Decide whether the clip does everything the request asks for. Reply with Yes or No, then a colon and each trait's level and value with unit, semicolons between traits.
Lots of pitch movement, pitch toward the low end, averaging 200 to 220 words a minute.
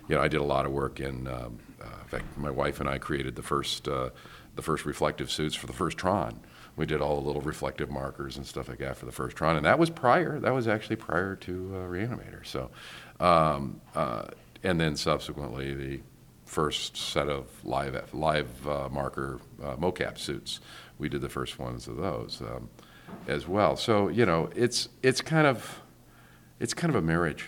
Yes: wide, 7.4 semitones; very low, 75 Hz; fast, 205 wpm